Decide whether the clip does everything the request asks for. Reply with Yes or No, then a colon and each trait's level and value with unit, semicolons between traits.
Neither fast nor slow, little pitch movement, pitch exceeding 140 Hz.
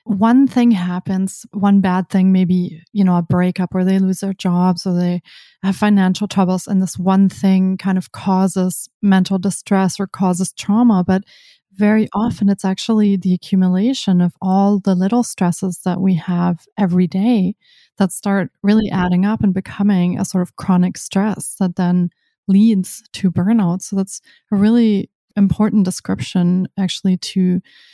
Yes: average, 160 wpm; narrow, 1.7 semitones; high, 190 Hz